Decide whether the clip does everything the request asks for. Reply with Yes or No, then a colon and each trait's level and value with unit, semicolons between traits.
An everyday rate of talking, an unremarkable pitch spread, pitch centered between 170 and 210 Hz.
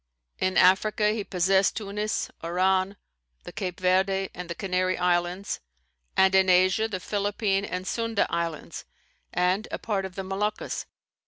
No: average, 145 wpm; narrow, 1.9 semitones; high, 190 Hz